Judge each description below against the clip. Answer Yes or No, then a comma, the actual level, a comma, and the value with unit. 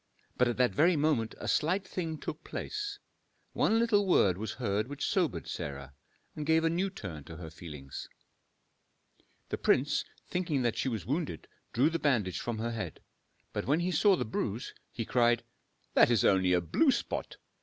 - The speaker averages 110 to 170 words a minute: No, average, 180 wpm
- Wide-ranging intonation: Yes, wide, 8.8 semitones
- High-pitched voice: No, low, 125 Hz